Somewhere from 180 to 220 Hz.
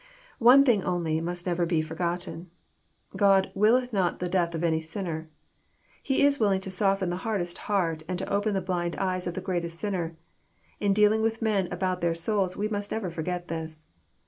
Yes: medium, 185 Hz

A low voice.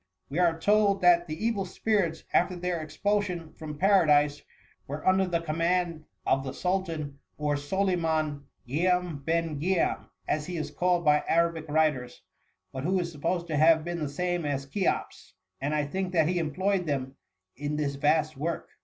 No: medium, 165 Hz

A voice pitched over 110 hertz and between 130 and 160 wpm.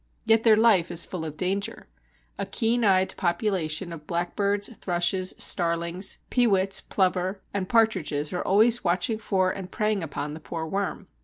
Yes: medium, 185 Hz; average, 155 wpm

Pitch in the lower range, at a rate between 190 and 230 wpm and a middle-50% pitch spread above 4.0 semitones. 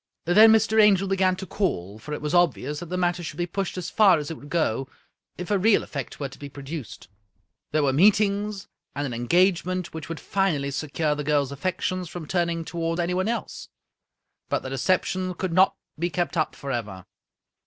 No: medium, 170 Hz; average, 195 wpm; average, 4.4 semitones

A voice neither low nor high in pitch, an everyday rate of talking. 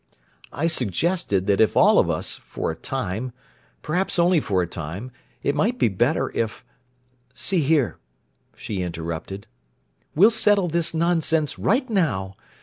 No: medium, 145 Hz; slow, 130 wpm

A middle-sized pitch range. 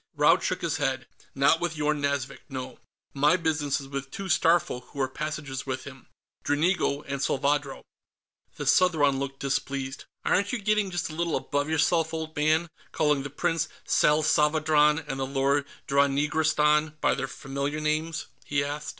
No: narrow, 2.3 semitones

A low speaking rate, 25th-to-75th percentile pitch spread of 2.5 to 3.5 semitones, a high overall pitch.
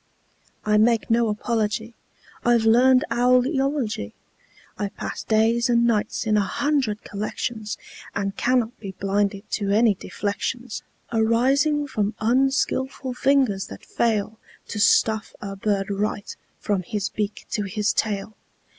Yes: slow, 130 wpm; average, 3.1 semitones; high, 220 Hz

